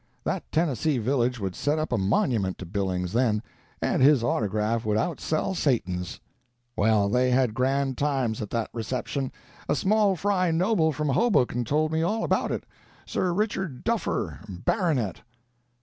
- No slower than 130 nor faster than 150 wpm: Yes, average, 145 wpm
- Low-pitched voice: Yes, low, 130 Hz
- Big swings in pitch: Yes, wide, 6.6 semitones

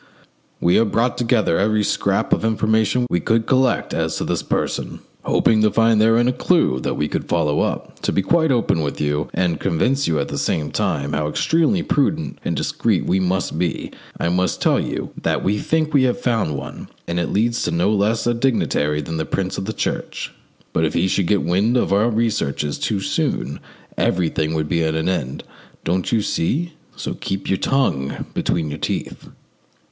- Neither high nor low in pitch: No, low, 100 Hz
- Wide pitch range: Yes, wide, 6.1 semitones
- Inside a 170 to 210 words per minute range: Yes, average, 200 wpm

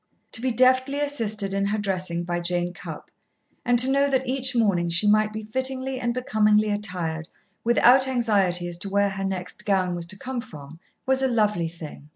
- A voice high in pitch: Yes, high, 210 Hz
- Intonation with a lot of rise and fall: Yes, wide, 6.0 semitones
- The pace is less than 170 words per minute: No, average, 195 wpm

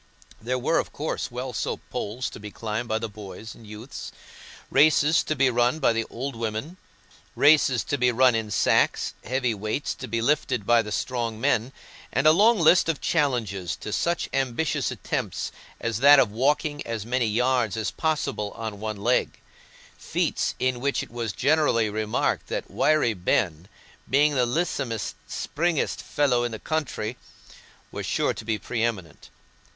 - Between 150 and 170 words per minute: Yes, average, 165 wpm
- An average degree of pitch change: Yes, average, 4.4 semitones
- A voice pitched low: Yes, low, 120 Hz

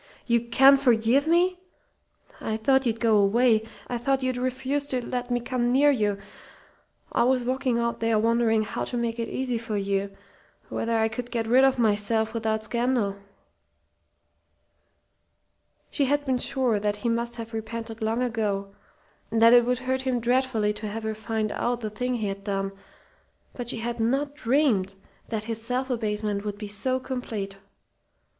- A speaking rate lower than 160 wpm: No, average, 175 wpm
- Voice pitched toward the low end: No, high, 235 Hz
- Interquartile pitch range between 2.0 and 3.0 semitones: Yes, narrow, 2.6 semitones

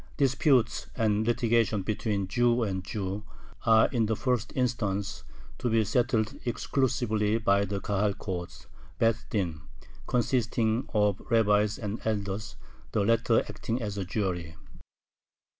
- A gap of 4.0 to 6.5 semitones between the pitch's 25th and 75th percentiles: No, average, 2.7 semitones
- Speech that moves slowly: Yes, slow, 125 wpm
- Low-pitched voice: Yes, low, 110 Hz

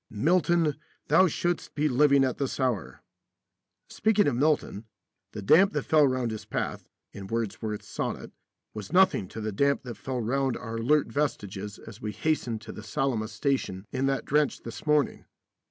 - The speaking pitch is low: Yes, low, 130 Hz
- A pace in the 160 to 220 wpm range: Yes, average, 170 wpm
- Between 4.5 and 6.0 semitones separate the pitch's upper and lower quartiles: Yes, wide, 5.4 semitones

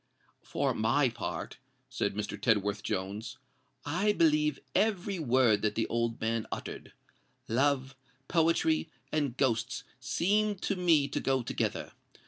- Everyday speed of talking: No, slow, 125 wpm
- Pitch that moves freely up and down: Yes, wide, 6.3 semitones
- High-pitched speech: No, low, 135 Hz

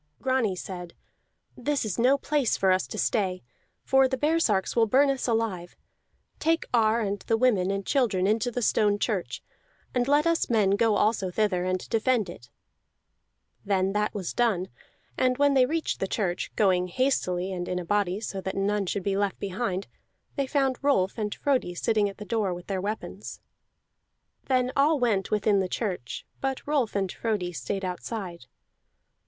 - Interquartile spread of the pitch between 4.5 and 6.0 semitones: Yes, average, 5.0 semitones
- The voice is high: Yes, high, 210 Hz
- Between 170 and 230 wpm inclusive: Yes, average, 175 wpm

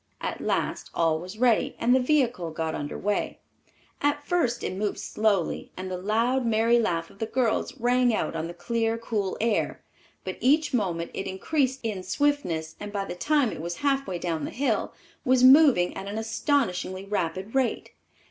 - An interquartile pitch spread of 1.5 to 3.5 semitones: No, wide, 5.5 semitones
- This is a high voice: Yes, high, 220 Hz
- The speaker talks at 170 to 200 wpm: Yes, average, 185 wpm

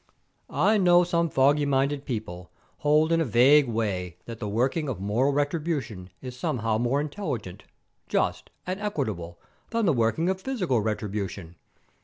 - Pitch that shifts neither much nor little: No, wide, 6.9 semitones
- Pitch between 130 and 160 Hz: Yes, low, 135 Hz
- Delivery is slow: No, average, 150 wpm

